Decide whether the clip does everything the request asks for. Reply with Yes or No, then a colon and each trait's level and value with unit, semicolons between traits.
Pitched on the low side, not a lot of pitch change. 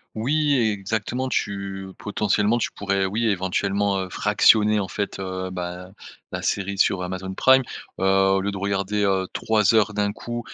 Yes: low, 100 Hz; narrow, 1.9 semitones